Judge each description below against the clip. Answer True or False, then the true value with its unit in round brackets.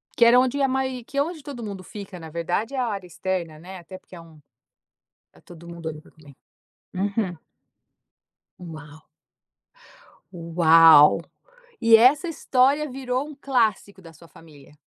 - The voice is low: False (190 Hz)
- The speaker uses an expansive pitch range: True (7.3 semitones)